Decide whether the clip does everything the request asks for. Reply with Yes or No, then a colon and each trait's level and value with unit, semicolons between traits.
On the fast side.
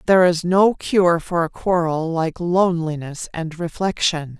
No: average, 150 wpm